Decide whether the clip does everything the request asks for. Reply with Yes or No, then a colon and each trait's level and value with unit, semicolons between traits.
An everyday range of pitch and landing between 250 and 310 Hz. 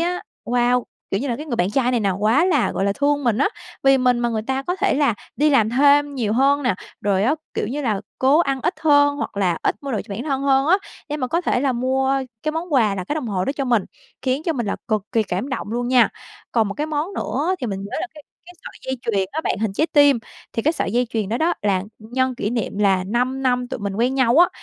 Yes: average, 4.8 semitones; very high, 255 Hz